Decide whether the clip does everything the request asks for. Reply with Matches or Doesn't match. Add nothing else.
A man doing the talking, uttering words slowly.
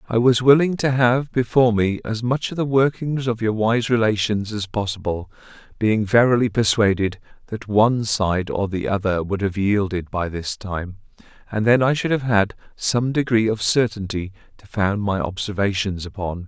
Doesn't match